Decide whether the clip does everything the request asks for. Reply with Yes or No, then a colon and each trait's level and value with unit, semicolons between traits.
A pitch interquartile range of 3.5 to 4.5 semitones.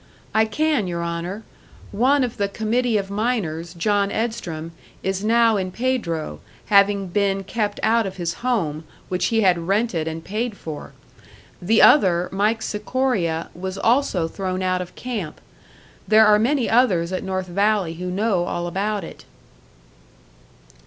Yes: average, 4.1 semitones